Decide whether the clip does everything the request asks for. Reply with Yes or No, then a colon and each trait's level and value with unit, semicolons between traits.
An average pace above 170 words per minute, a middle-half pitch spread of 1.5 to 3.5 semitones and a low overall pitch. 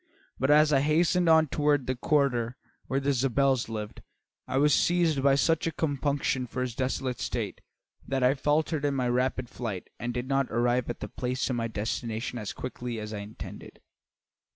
Yes: average, 180 wpm; average, 3.1 semitones; low, 130 Hz